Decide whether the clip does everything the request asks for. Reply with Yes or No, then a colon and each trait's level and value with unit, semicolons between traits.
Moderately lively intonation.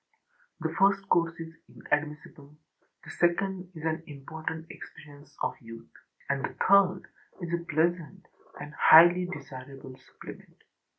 Yes: average, 3.2 semitones